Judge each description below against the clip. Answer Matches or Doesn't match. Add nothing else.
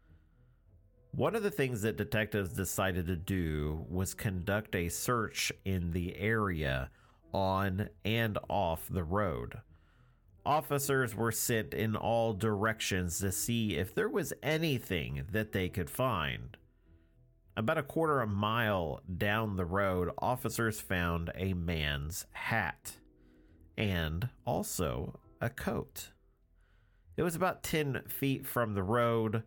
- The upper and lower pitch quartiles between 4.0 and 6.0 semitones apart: Matches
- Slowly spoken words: Matches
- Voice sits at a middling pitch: Doesn't match